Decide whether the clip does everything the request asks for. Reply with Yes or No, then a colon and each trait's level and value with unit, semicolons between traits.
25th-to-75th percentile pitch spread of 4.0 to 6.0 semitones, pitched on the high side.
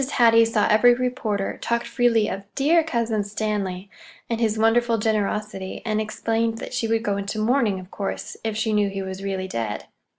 No: narrow, 2.5 semitones; high, 215 Hz